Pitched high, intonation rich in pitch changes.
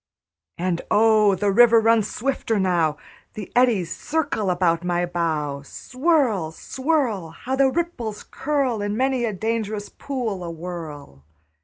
Yes: high, 210 Hz; wide, 6.1 semitones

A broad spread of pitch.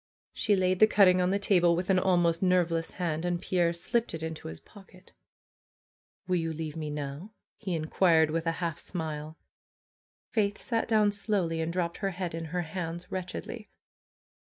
No: average, 2.7 semitones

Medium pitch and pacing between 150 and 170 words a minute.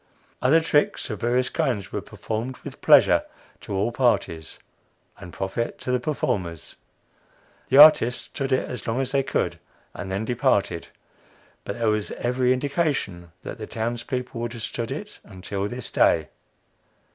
No: low, 120 Hz; average, 155 wpm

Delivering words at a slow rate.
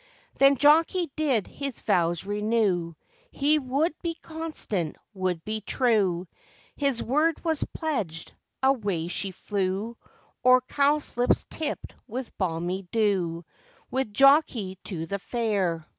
Yes: slow, 115 wpm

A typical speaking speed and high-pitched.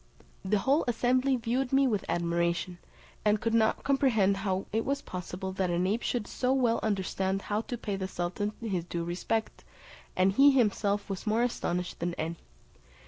Yes: average, 175 wpm; high, 205 Hz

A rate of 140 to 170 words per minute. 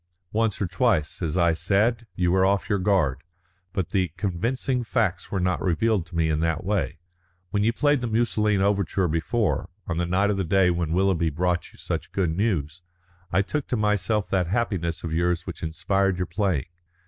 No: average, 195 wpm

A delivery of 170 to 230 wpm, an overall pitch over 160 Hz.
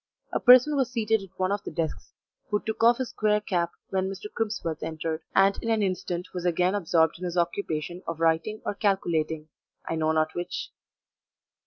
Yes: average, 190 wpm; medium, 185 Hz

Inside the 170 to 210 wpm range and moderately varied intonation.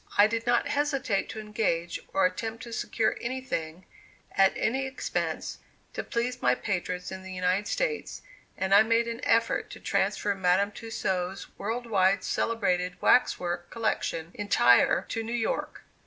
No: average, 155 wpm; average, 4.0 semitones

